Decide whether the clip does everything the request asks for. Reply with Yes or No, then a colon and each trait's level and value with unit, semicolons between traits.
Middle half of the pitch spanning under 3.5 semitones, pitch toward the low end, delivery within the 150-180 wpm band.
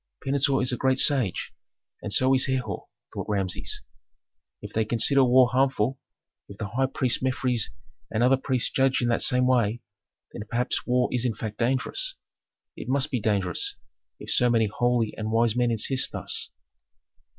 Yes: average, 2.9 semitones; low, 125 Hz; average, 170 wpm